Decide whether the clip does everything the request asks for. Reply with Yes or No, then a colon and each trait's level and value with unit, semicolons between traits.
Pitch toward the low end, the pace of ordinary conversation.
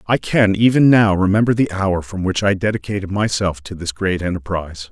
Yes: low, 100 Hz; average, 195 wpm